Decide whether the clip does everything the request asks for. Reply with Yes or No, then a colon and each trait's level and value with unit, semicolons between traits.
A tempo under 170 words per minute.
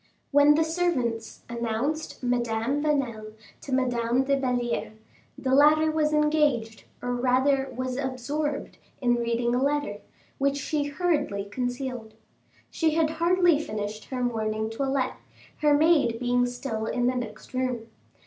Yes: slow, 135 wpm